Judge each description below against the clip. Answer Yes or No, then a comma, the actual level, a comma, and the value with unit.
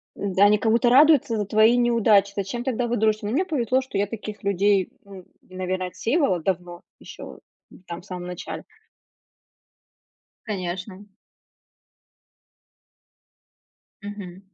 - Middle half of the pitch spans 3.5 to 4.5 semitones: Yes, average, 3.9 semitones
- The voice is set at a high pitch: Yes, high, 205 Hz